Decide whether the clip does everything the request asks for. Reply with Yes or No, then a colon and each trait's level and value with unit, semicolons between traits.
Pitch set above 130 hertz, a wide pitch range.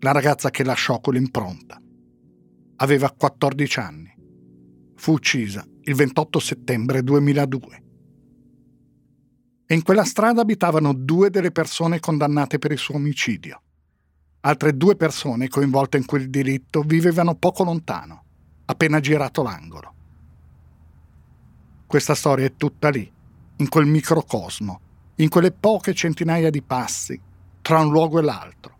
Yes: medium, 140 Hz; wide, 7.7 semitones